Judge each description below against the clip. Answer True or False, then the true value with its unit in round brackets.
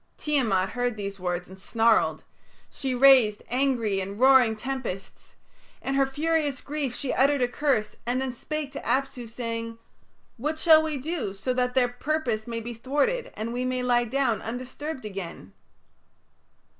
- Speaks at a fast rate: False (155 wpm)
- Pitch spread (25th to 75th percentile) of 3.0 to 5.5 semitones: True (3.6 semitones)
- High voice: True (250 Hz)